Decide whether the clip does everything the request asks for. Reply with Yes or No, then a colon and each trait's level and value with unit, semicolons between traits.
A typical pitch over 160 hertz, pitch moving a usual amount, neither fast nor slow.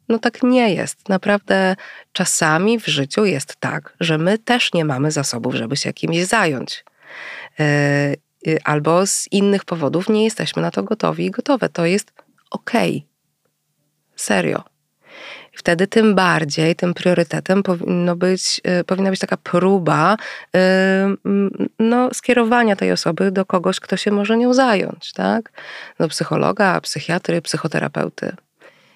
Yes: medium, 185 Hz; average, 4.3 semitones; average, 130 wpm